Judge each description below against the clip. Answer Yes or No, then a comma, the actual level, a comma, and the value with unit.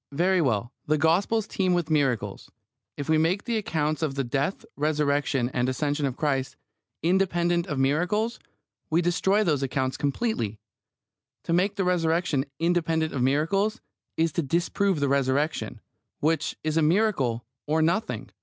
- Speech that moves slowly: No, average, 150 wpm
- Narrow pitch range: No, average, 4.1 semitones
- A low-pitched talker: No, medium, 160 Hz